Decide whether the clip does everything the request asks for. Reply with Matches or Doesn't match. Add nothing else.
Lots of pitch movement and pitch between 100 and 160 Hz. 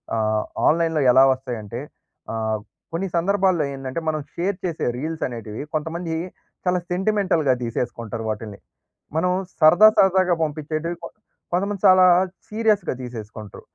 Matches